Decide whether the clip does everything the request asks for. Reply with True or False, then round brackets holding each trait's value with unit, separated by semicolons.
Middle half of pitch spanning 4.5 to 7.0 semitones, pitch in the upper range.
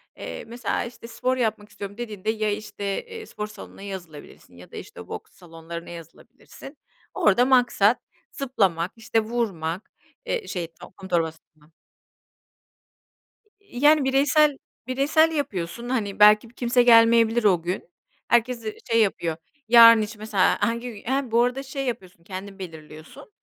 True (4.9 semitones; 220 Hz)